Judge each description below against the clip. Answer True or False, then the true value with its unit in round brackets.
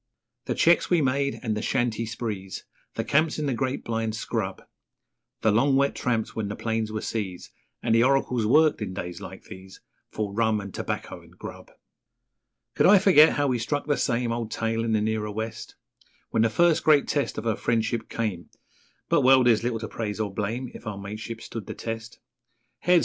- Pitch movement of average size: True (3.4 semitones)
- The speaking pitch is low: True (115 Hz)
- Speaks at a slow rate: False (200 wpm)